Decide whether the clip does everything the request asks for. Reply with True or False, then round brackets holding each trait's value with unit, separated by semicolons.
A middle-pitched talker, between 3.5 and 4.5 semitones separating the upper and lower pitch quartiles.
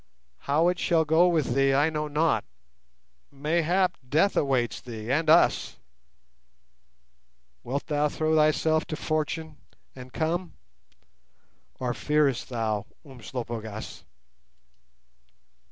True (150 Hz; 4.0 semitones)